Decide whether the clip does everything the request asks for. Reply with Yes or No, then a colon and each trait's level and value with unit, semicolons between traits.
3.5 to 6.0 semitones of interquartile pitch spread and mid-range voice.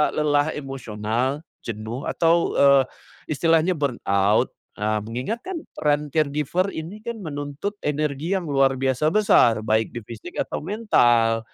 Yes: average, 5.3 semitones; medium, 145 Hz